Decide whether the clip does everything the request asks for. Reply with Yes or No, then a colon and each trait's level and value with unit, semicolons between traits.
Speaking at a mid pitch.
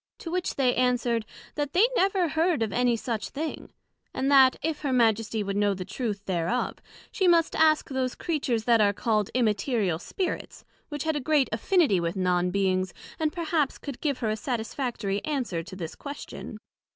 No: high, 245 Hz